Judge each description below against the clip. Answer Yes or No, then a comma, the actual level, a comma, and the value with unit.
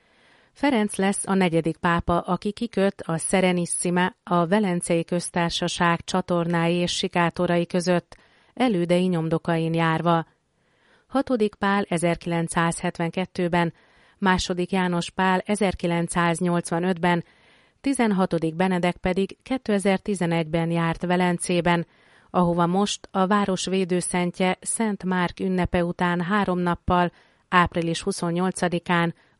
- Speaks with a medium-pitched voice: Yes, medium, 180 Hz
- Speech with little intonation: Yes, narrow, 1.7 semitones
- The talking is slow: Yes, slow, 90 wpm